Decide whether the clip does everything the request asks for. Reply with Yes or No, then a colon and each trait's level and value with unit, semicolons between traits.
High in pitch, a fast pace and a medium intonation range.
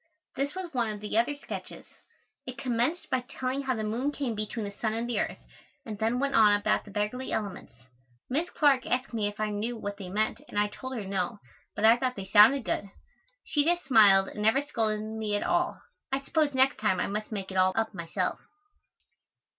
Yes: high, 220 Hz; fast, 215 wpm; average, 4.0 semitones